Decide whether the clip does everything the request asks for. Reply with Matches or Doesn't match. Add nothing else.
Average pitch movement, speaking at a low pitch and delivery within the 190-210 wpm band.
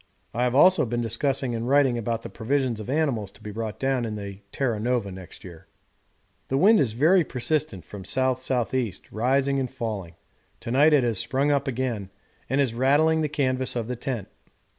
Matches